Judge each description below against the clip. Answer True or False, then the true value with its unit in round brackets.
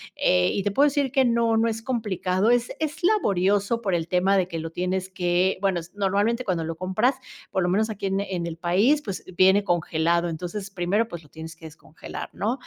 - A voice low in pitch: False (190 Hz)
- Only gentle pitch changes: False (4.3 semitones)